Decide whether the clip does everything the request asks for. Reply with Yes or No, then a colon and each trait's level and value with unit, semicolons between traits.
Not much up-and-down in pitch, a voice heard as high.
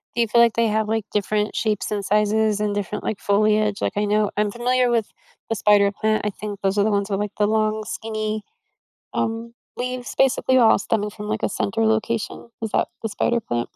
Yes: narrow, 1.4 semitones; high, 215 Hz